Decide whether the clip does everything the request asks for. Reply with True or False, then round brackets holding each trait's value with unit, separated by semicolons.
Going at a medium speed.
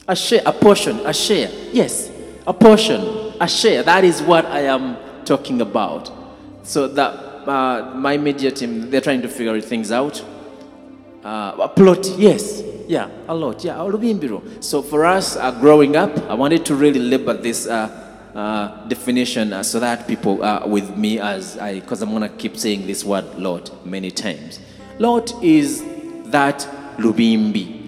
True (170 wpm)